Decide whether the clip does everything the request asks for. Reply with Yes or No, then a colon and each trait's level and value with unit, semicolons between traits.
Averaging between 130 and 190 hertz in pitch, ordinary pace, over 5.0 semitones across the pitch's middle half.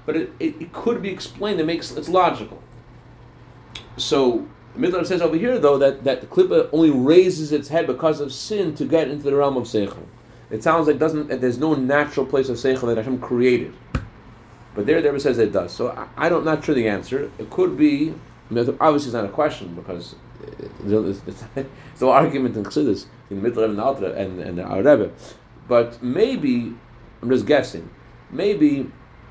Yes: medium, 140 Hz; average, 190 wpm; wide, 5.6 semitones